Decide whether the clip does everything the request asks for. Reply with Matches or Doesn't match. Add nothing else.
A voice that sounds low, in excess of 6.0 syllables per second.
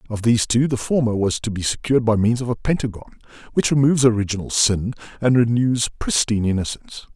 Matches